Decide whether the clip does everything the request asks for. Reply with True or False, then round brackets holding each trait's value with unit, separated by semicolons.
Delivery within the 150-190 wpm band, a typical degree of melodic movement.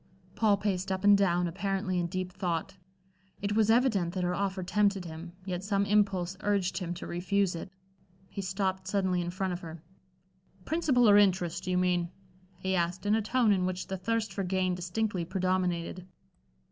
False (185 wpm; 2.1 semitones)